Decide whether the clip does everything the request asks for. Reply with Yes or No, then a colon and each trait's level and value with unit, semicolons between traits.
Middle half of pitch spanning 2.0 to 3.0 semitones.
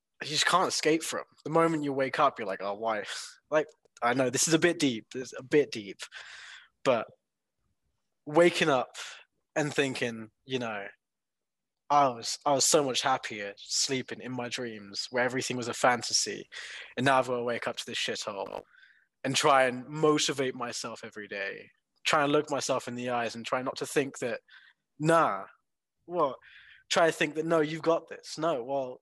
No: average, 4.0 semitones